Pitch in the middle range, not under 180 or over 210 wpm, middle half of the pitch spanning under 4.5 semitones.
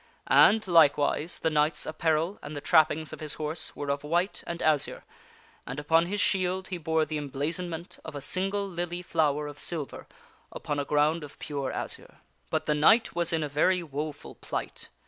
Yes: medium, 155 Hz; average, 185 wpm; average, 2.8 semitones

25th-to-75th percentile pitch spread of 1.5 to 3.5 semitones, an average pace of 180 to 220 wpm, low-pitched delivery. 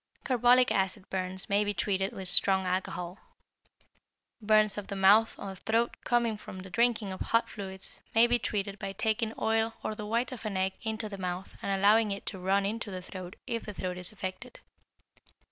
No: average, 2.8 semitones; average, 195 wpm; high, 200 Hz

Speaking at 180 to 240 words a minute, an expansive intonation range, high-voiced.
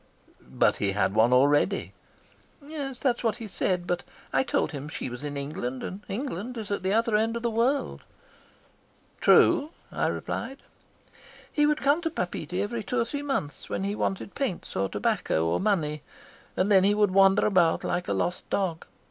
Yes: average, 185 wpm; wide, 7.6 semitones; high, 195 Hz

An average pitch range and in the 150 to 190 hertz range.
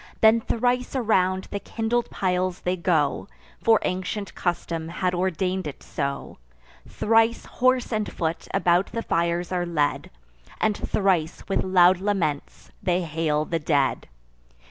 Yes: average, 4.0 semitones; medium, 185 Hz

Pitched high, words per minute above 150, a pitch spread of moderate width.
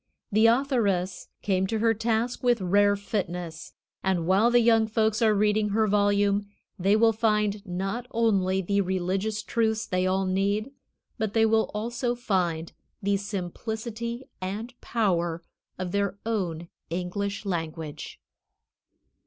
No: high, 205 Hz; slow, 135 wpm; average, 3.0 semitones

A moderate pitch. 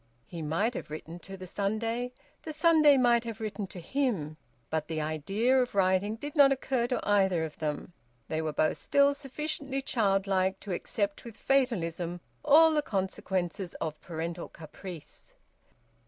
No: high, 200 Hz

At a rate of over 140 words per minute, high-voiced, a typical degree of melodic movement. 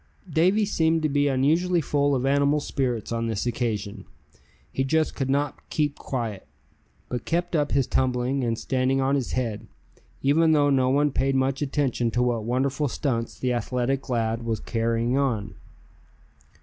No: average, 160 wpm; low, 135 Hz; average, 3.1 semitones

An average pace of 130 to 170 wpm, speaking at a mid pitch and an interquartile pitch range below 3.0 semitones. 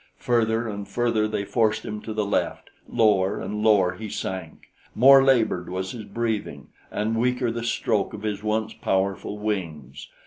No: average, 165 wpm; low, 105 Hz; narrow, 2.5 semitones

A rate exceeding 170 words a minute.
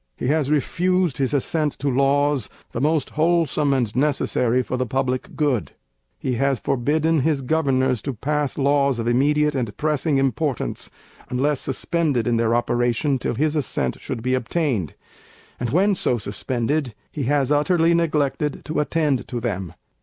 No: average, 155 wpm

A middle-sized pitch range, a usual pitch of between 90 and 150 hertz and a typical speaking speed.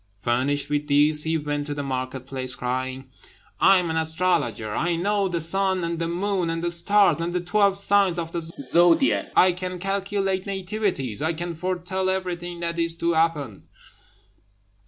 No: average, 4.1 semitones; medium, 170 Hz; average, 175 wpm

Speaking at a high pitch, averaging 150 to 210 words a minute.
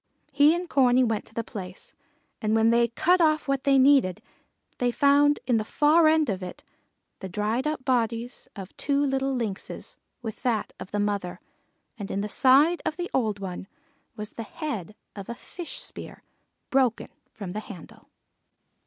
Yes: high, 240 Hz; average, 175 wpm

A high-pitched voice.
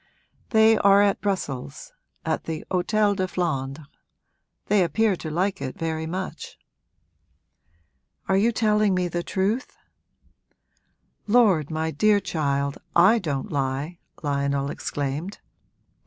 No: medium, 180 Hz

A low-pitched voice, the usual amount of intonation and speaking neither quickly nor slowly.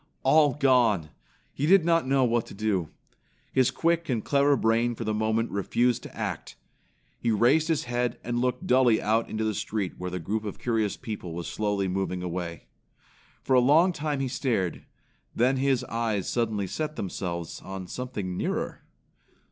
Yes: low, 115 Hz; average, 4.7 semitones; average, 170 wpm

